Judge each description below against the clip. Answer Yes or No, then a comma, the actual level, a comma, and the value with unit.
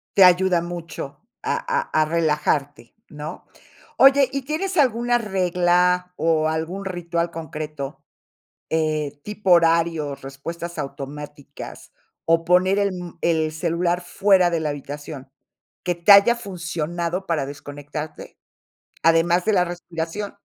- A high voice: No, medium, 170 Hz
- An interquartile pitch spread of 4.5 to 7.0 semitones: No, average, 3.0 semitones